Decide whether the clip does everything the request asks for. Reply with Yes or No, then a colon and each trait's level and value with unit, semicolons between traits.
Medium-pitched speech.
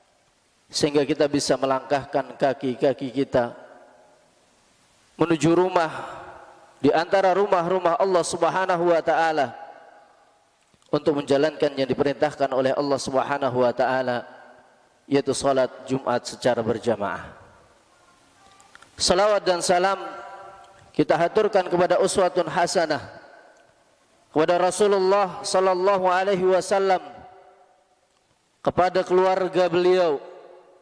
Yes: medium, 170 Hz